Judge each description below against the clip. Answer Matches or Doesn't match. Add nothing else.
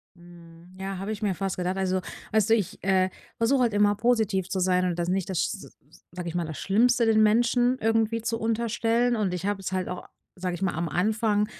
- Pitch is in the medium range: Doesn't match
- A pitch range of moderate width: Matches